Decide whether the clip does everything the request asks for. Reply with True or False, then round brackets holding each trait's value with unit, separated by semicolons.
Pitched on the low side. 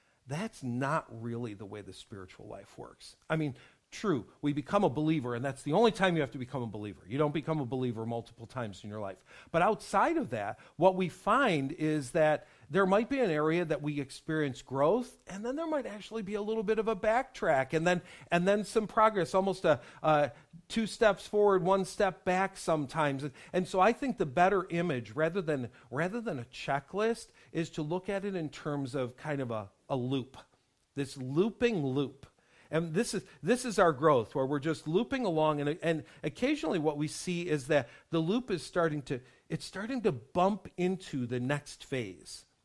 False (160 Hz)